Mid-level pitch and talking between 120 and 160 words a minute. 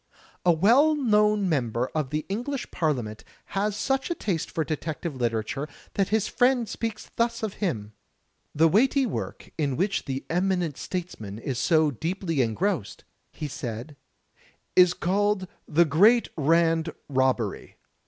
Yes: medium, 170 Hz; average, 140 wpm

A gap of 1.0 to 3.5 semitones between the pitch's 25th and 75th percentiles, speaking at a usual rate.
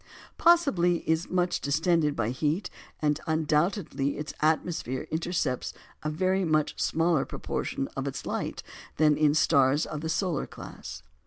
Yes: average, 3.2 semitones; average, 145 wpm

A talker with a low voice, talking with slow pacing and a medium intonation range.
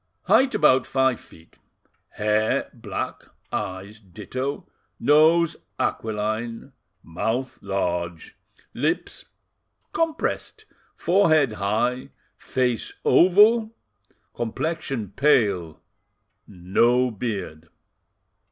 No: low, 120 Hz; slow, 70 wpm; wide, 6.3 semitones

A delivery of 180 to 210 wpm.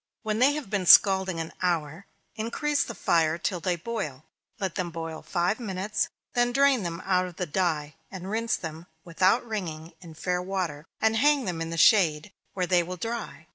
Yes: average, 190 wpm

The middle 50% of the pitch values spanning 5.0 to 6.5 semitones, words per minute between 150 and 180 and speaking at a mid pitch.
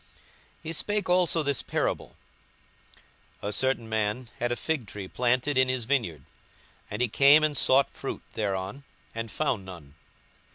No: average, 5.3 semitones; average, 155 wpm; low, 125 Hz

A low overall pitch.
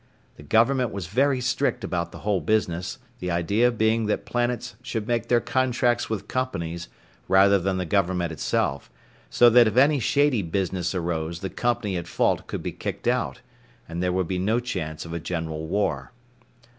Yes: low, 100 Hz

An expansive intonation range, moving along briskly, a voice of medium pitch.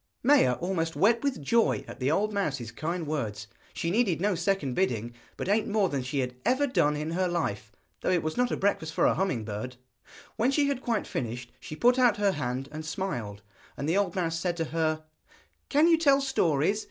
Yes: wide, 7.1 semitones; fast, 215 wpm; medium, 170 Hz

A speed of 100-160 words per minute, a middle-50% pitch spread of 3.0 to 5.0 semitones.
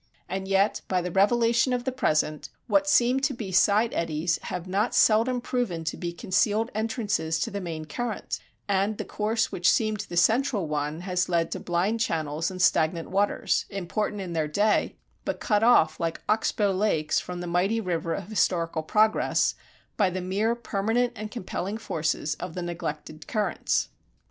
No: average, 175 wpm; average, 4.4 semitones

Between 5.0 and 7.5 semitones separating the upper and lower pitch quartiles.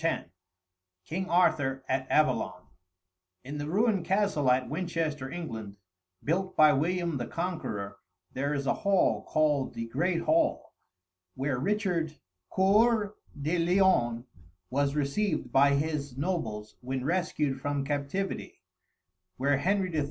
Yes: average, 5.3 semitones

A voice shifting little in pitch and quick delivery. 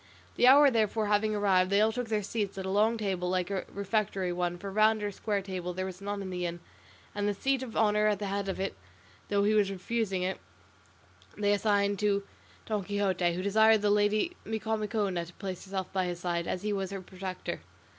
Yes: narrow, 2.2 semitones; fast, 220 wpm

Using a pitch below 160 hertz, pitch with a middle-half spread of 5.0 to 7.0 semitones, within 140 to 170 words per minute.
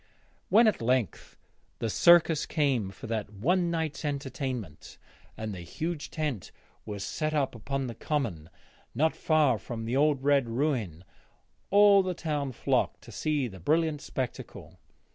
Yes: medium, 140 Hz; wide, 5.6 semitones; average, 145 wpm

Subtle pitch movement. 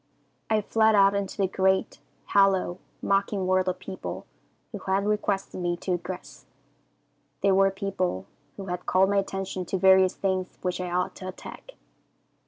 Yes: narrow, 1.2 semitones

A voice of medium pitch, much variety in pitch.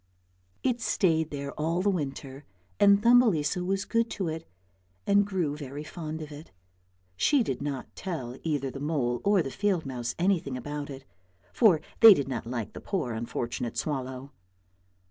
Yes: medium, 150 Hz; wide, 6.1 semitones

